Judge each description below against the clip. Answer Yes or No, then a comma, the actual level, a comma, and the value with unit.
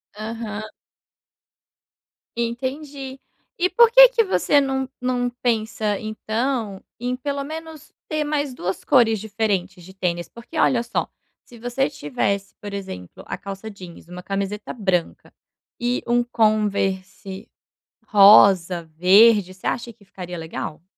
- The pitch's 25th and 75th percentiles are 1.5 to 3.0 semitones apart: No, average, 4.7 semitones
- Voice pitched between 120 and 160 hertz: No, high, 220 Hz